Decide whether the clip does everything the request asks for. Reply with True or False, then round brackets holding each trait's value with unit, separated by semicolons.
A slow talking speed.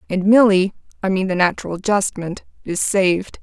True (125 wpm)